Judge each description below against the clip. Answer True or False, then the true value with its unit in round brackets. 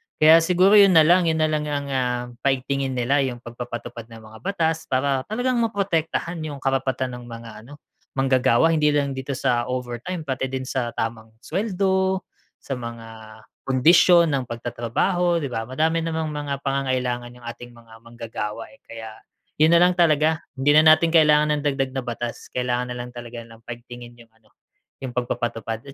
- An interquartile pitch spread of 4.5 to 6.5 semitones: True (4.8 semitones)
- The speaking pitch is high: False (135 Hz)